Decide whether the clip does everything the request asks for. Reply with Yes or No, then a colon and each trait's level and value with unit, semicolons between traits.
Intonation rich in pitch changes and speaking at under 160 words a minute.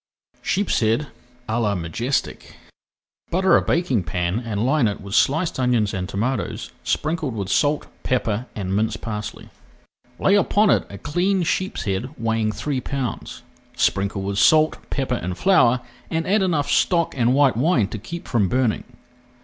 Yes: wide, 6.7 semitones; average, 150 wpm